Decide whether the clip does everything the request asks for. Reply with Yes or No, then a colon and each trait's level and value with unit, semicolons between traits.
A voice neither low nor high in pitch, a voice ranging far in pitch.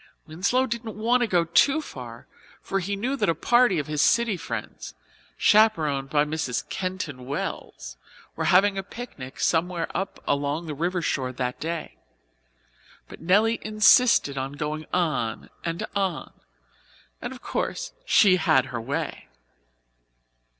Yes: medium, 170 Hz; wide, 6.2 semitones